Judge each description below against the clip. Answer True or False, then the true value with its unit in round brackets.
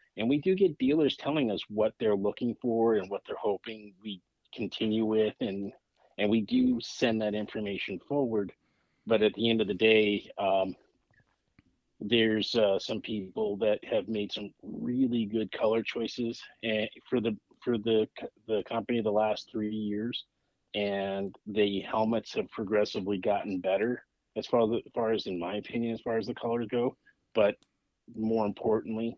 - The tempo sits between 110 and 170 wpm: True (160 wpm)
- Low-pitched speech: True (110 Hz)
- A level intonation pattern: True (1.8 semitones)